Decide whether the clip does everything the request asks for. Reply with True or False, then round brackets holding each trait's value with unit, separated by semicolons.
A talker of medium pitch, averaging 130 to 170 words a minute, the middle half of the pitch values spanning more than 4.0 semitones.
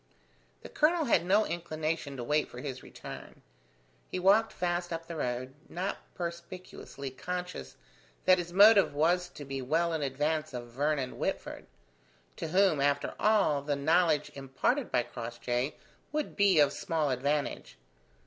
True (155 Hz; 150 wpm; 4.5 semitones)